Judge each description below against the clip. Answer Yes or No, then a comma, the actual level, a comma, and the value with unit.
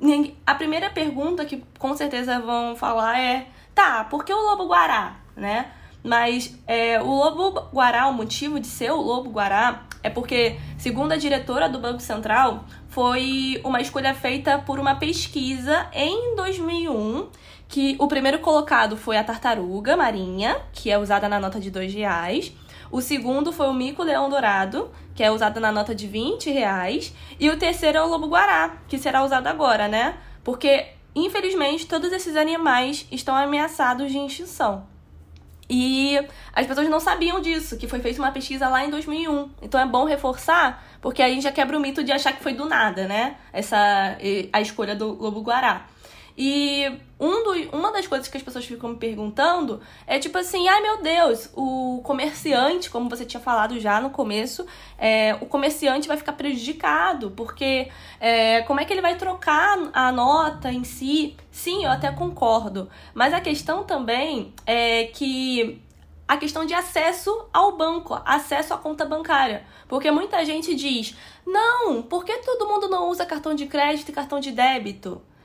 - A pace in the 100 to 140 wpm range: No, average, 170 wpm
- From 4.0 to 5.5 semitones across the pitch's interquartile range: Yes, average, 4.6 semitones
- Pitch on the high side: Yes, very high, 275 Hz